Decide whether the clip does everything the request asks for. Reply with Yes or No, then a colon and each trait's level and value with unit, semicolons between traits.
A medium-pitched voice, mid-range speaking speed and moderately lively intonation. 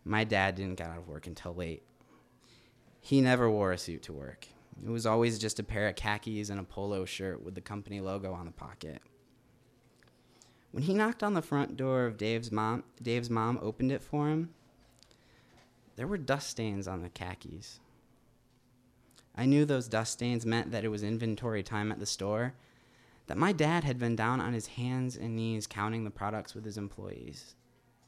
No: low, 115 Hz; average, 190 wpm; average, 3.3 semitones